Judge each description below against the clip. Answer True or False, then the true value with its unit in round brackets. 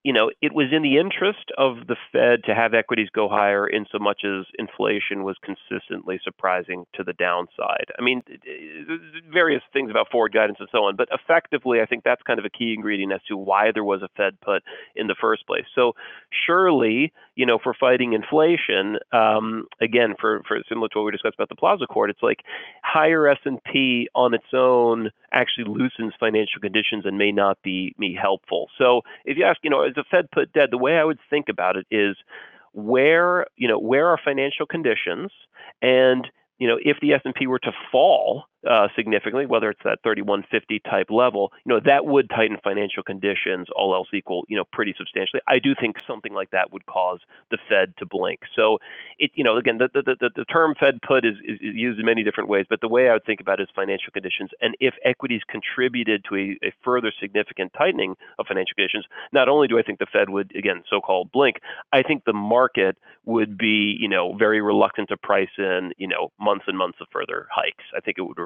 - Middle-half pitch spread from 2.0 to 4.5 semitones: False (5.4 semitones)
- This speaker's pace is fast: True (215 wpm)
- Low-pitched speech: True (120 Hz)